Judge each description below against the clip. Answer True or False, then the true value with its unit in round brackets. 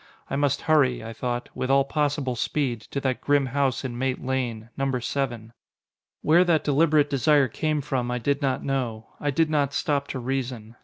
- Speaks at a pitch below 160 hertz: True (135 Hz)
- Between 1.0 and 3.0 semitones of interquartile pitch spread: True (2.7 semitones)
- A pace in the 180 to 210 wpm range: True (190 wpm)